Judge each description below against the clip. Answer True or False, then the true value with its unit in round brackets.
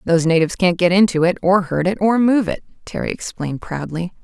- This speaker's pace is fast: True (210 wpm)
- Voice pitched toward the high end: False (180 Hz)